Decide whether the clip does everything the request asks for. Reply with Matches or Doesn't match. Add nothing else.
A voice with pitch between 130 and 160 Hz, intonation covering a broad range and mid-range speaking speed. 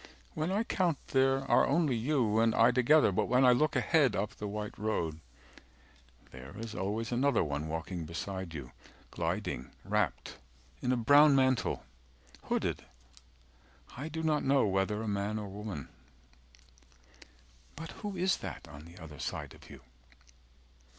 Doesn't match